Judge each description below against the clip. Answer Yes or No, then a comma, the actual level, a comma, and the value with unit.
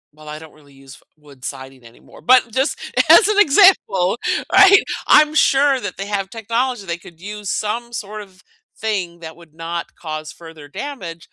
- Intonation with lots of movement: Yes, wide, 7.3 semitones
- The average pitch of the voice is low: No, high, 190 Hz